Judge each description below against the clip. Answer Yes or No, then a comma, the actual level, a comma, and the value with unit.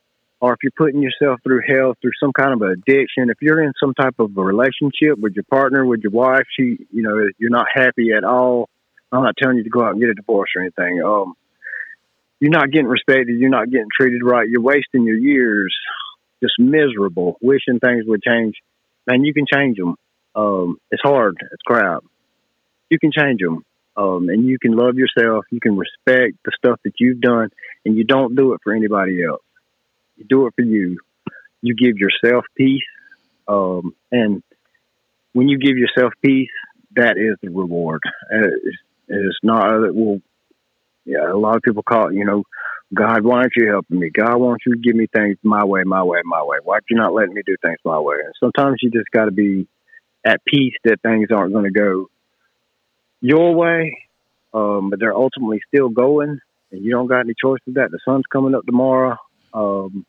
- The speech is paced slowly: No, fast, 205 wpm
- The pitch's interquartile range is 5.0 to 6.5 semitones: No, average, 4.0 semitones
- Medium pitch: No, low, 120 Hz